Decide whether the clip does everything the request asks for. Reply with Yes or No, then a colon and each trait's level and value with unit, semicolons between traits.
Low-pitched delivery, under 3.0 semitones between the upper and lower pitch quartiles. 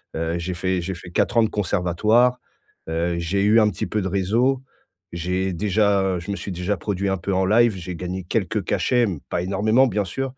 No: very low, 95 Hz; average, 3.3 semitones